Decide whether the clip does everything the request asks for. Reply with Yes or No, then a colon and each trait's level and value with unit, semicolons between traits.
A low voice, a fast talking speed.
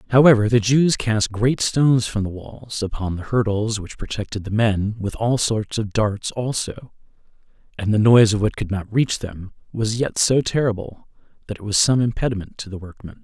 No: low, 110 Hz; average, 195 wpm